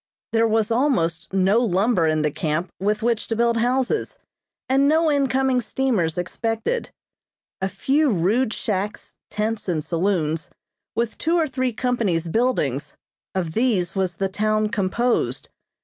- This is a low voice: No, high, 215 Hz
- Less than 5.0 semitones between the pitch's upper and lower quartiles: No, wide, 5.6 semitones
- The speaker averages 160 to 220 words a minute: No, average, 140 wpm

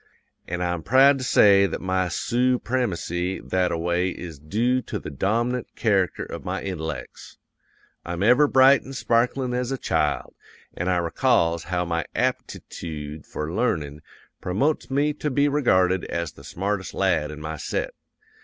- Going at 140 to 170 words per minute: Yes, average, 155 wpm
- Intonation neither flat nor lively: No, wide, 6.8 semitones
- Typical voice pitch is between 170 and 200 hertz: No, very low, 95 Hz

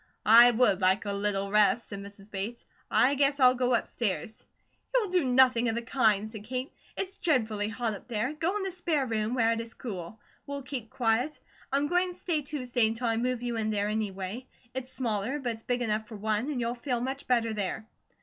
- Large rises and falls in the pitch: No, average, 3.4 semitones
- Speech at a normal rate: No, fast, 215 wpm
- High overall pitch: Yes, high, 235 Hz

